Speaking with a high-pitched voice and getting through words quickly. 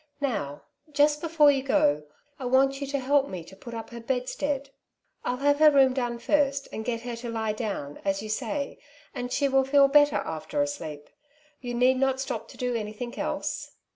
Yes: very high, 260 Hz; fast, 210 wpm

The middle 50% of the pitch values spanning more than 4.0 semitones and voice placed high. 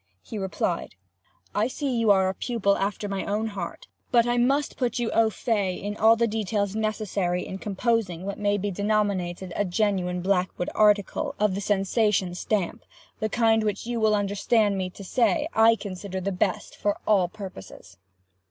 No: average, 2.7 semitones; high, 205 Hz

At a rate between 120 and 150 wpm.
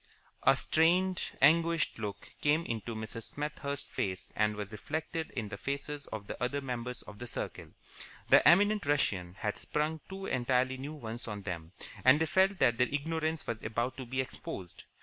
No: average, 175 wpm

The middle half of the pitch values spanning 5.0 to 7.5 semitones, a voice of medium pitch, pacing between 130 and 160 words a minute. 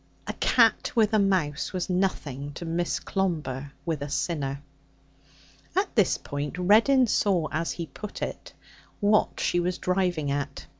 Yes: average, 5.3 semitones; medium, 175 Hz; average, 150 wpm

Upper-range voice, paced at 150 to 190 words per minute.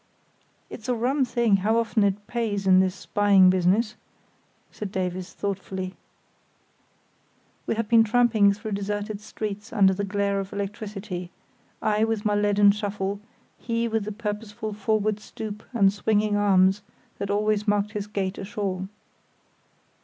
No: high, 205 Hz; average, 140 wpm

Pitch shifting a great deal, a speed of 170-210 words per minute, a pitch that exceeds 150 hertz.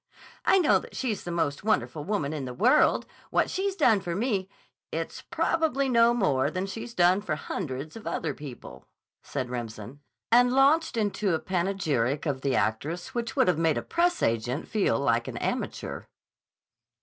Yes: wide, 8.6 semitones; average, 175 wpm; medium, 185 Hz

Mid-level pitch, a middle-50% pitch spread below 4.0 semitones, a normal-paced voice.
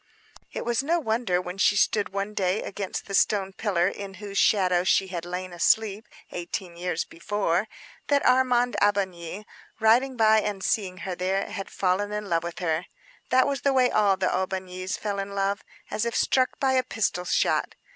No: high, 200 Hz; average, 3.2 semitones; average, 185 wpm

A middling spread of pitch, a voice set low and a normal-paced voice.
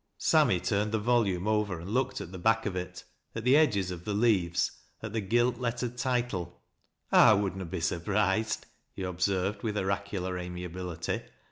Yes: average, 3.6 semitones; low, 100 Hz; average, 175 wpm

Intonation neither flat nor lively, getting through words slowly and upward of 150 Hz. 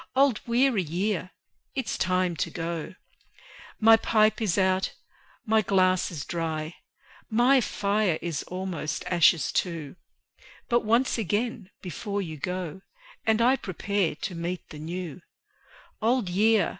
Yes: average, 4.4 semitones; slow, 130 wpm; medium, 185 Hz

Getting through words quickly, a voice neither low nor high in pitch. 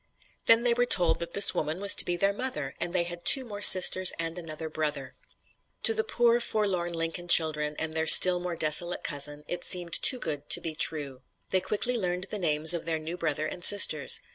Yes: fast, 215 wpm; medium, 175 Hz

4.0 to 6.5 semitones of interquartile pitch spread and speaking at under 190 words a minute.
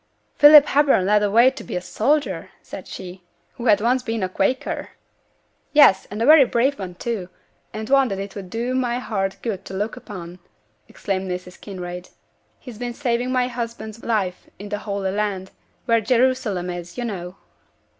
Yes: average, 4.5 semitones; average, 175 wpm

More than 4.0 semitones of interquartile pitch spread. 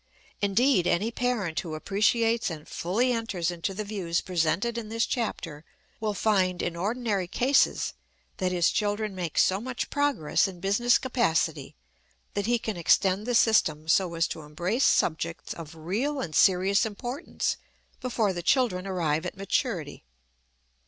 Yes: average, 4.9 semitones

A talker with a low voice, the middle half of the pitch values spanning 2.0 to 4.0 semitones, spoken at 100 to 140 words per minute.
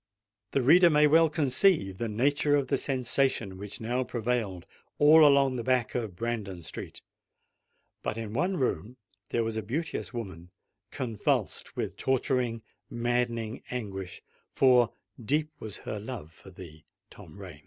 No: low, 120 Hz; average, 4.8 semitones; slow, 135 wpm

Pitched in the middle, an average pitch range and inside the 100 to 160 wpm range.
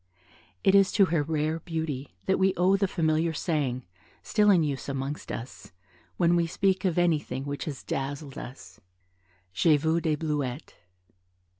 Yes: medium, 160 Hz; average, 3.7 semitones; average, 155 wpm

